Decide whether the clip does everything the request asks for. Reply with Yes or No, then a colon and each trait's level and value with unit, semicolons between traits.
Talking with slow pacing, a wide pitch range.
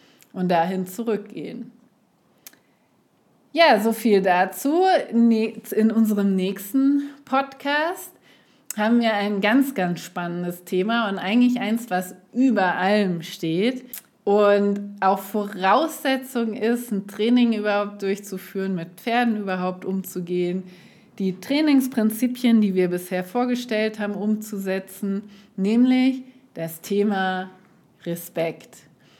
No: slow, 100 wpm; average, 4.2 semitones